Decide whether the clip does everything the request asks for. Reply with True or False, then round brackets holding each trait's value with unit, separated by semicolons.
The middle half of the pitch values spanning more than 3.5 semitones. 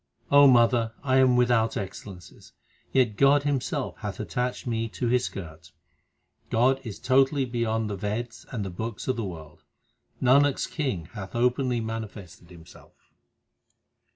True (3.9 semitones)